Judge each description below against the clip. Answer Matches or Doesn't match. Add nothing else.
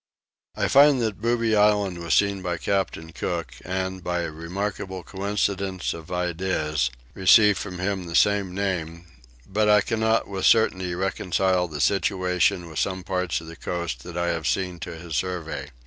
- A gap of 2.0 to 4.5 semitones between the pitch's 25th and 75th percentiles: Matches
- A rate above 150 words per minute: Matches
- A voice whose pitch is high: Doesn't match